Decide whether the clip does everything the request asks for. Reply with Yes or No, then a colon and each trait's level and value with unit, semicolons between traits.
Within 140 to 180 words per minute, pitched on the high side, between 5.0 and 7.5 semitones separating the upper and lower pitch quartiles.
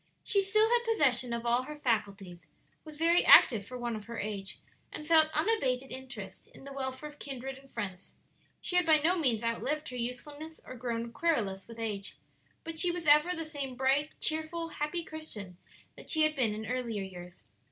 No: average, 190 wpm; very high, 265 Hz; average, 5.3 semitones